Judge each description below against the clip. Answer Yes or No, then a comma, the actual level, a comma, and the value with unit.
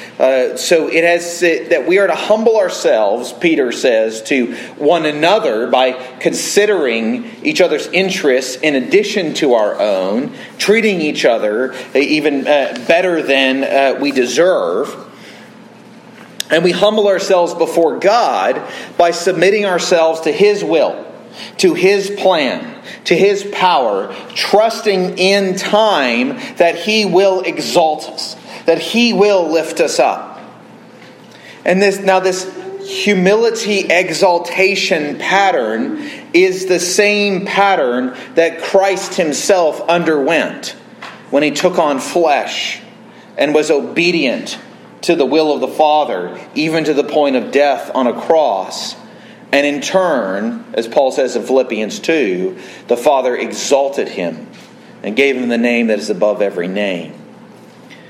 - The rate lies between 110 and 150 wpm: Yes, slow, 135 wpm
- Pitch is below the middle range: No, medium, 185 Hz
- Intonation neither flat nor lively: No, wide, 6.2 semitones